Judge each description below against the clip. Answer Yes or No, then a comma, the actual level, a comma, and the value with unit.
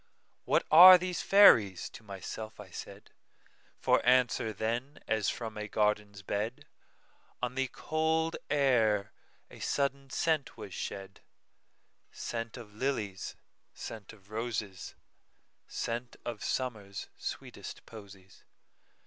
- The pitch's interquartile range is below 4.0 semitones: No, average, 4.3 semitones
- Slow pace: Yes, slow, 100 wpm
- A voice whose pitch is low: Yes, low, 115 Hz